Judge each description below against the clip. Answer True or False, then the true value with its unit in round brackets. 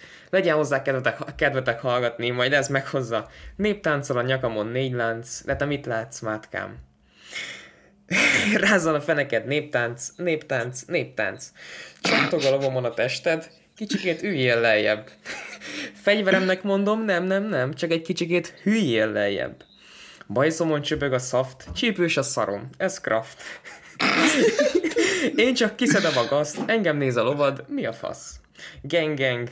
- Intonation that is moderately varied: False (7.0 semitones)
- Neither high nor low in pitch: True (145 Hz)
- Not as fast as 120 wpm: False (130 wpm)